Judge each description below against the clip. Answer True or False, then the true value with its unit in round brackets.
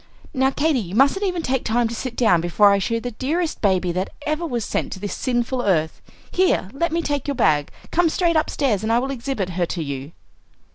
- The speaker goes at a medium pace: False (230 wpm)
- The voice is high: True (240 Hz)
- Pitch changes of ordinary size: False (7.1 semitones)